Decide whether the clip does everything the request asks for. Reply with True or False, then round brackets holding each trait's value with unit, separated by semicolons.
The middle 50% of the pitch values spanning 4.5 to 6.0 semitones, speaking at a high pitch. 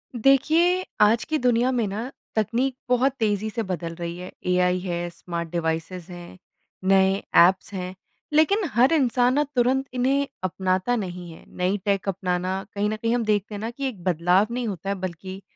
True (5.3 semitones; 200 Hz)